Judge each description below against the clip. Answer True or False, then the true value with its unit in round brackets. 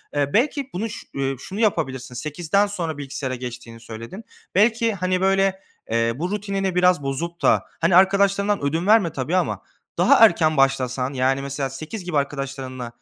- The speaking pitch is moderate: True (160 Hz)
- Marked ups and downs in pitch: True (6.4 semitones)